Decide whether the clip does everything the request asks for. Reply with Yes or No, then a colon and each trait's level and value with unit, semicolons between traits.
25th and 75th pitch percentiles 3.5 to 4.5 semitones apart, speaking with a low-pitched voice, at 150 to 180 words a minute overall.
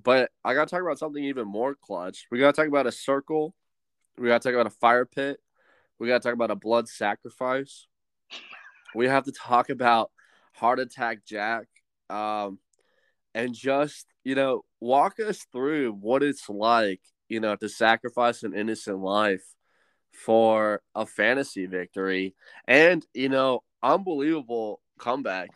Yes: average, 3.9 semitones; low, 120 Hz; average, 160 wpm